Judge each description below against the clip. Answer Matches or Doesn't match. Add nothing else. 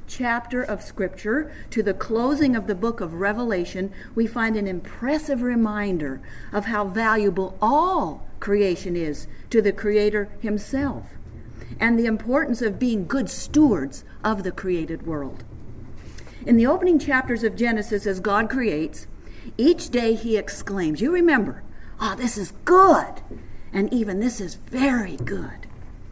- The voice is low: Doesn't match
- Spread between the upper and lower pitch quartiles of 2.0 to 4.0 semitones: Doesn't match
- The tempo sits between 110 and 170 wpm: Matches